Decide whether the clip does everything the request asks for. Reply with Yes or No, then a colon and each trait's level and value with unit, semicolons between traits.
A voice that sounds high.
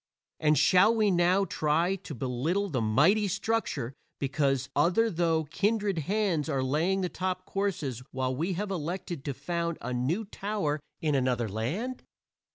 No: medium, 170 Hz